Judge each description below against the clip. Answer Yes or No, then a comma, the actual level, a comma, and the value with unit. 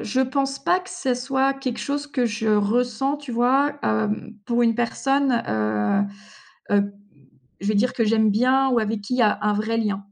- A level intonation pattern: No, average, 4.2 semitones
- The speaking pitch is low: No, high, 240 Hz